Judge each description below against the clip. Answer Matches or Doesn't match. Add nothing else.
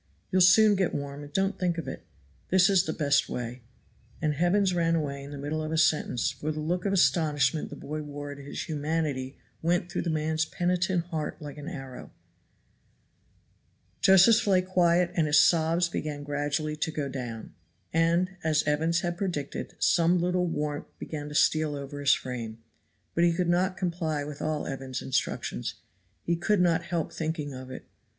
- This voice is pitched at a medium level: Matches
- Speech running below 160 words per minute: Doesn't match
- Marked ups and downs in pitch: Doesn't match